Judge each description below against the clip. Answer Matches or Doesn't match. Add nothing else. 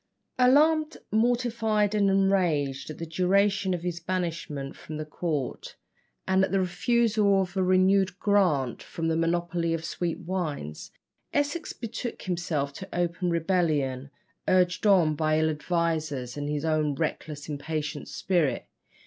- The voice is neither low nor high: Matches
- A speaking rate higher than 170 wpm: Doesn't match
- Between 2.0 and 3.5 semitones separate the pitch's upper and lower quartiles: Doesn't match